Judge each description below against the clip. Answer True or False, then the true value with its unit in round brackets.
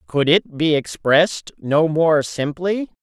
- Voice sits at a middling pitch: True (155 Hz)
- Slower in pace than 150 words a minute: True (140 wpm)